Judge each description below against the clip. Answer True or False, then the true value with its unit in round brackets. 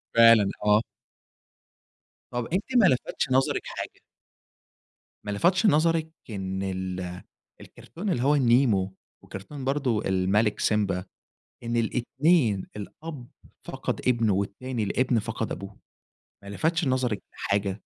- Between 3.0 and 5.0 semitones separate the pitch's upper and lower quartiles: False (5.4 semitones)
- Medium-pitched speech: False (115 Hz)